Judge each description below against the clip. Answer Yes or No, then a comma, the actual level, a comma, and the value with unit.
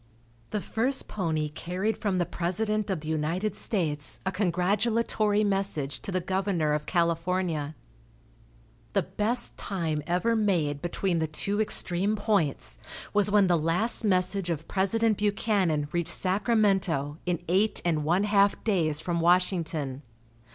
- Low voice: No, medium, 185 Hz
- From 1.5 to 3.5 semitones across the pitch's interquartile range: No, average, 4.0 semitones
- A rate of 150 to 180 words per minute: No, slow, 135 wpm